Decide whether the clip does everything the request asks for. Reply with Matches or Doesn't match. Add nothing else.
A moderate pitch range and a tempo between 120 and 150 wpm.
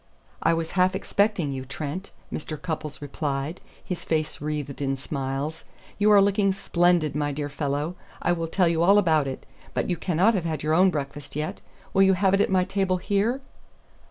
Doesn't match